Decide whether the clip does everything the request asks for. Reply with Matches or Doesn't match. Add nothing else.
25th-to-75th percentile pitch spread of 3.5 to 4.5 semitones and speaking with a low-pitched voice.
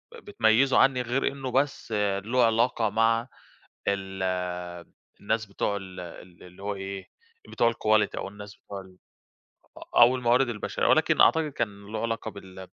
Matches